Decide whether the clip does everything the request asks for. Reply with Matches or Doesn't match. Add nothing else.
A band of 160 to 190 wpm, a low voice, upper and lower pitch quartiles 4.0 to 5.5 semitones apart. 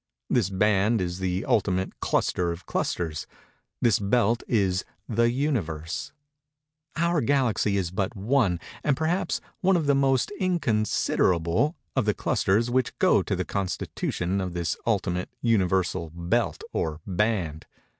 Doesn't match